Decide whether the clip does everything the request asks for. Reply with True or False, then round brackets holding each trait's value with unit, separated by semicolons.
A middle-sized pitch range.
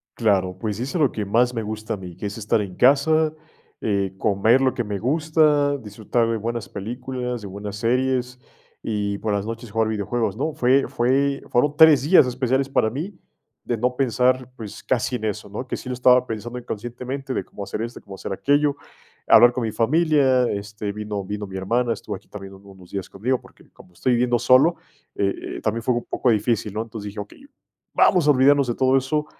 True (4.0 semitones)